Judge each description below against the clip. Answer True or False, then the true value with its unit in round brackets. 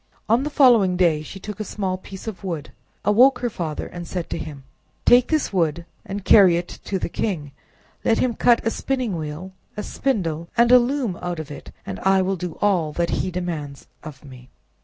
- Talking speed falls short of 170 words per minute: False (205 wpm)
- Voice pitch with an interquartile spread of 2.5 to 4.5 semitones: False (5.3 semitones)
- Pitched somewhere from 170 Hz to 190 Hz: True (185 Hz)